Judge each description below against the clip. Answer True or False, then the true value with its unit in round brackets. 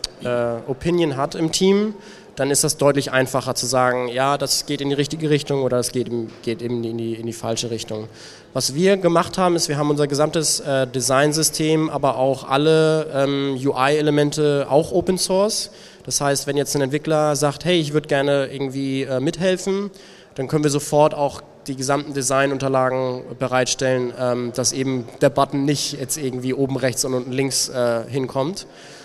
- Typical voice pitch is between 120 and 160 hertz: True (140 Hz)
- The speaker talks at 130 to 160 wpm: False (180 wpm)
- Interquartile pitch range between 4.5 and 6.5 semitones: False (2.9 semitones)